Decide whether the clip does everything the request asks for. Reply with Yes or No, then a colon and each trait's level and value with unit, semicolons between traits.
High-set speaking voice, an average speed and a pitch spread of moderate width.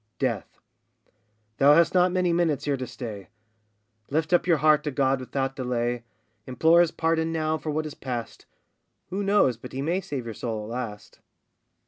No: medium, 145 Hz; average, 175 wpm; average, 4.6 semitones